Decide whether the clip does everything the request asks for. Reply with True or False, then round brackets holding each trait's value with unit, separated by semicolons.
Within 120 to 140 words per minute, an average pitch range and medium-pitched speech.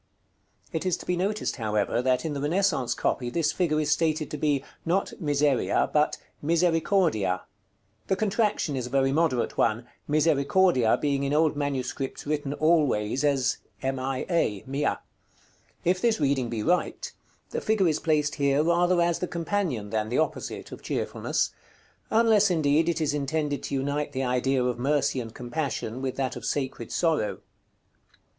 False (155 wpm; 4.3 semitones; 145 Hz)